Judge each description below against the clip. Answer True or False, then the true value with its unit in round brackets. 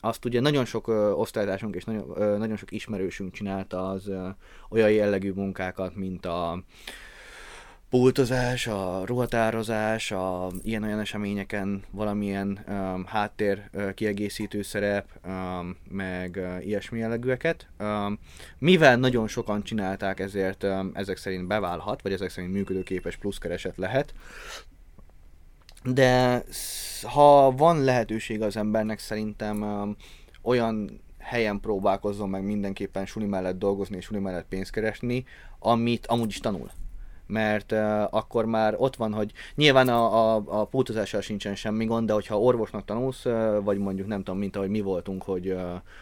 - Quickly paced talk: False (135 wpm)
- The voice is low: True (105 Hz)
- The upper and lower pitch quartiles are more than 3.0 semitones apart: False (2.7 semitones)